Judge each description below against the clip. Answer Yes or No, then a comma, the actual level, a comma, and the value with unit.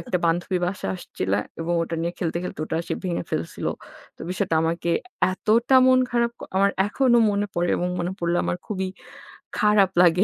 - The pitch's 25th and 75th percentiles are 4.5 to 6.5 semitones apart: No, average, 3.3 semitones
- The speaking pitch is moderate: Yes, medium, 180 Hz